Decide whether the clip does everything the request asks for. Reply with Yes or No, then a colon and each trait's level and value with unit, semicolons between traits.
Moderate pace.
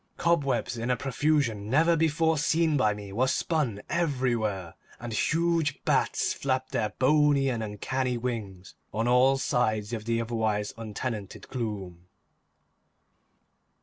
No: slow, 125 wpm